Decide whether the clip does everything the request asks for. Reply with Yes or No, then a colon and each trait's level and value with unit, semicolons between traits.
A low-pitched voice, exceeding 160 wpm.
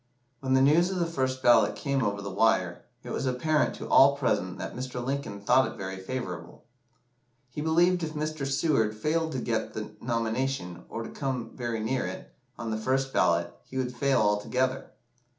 Yes: low, 130 Hz; average, 185 wpm